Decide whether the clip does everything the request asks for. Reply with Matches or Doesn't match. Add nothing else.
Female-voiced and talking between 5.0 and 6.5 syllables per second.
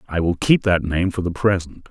Doesn't match